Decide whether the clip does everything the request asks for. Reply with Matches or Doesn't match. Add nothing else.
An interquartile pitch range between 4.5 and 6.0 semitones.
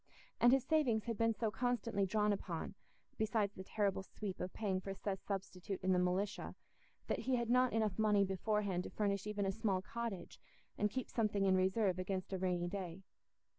Doesn't match